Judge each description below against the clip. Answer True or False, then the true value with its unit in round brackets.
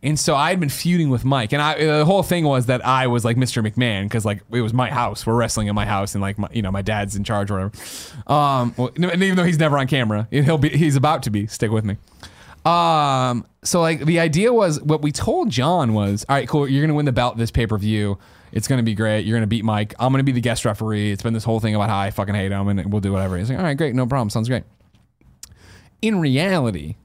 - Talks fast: True (270 wpm)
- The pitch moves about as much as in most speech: False (5.8 semitones)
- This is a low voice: True (120 Hz)